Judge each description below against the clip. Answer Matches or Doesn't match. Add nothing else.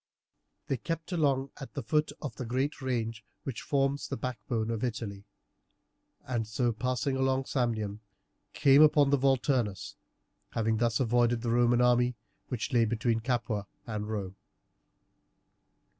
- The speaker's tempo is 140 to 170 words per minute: Matches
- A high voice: Doesn't match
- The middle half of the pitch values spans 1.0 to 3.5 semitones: Matches